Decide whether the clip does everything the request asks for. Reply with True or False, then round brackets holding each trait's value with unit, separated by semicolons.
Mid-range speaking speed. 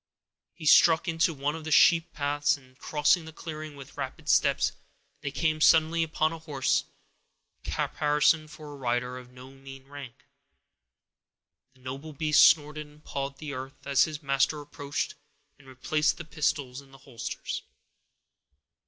True (155 wpm)